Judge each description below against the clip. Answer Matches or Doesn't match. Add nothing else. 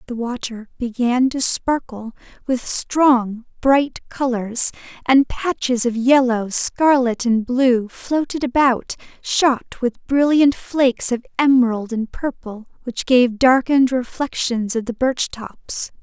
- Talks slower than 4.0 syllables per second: Matches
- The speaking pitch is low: Doesn't match